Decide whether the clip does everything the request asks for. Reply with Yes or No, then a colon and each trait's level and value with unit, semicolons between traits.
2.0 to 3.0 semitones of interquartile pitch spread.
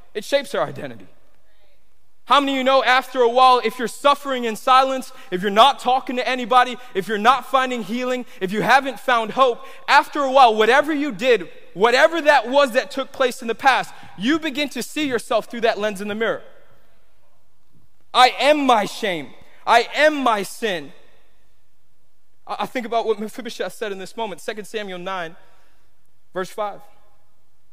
No: average, 4.3 semitones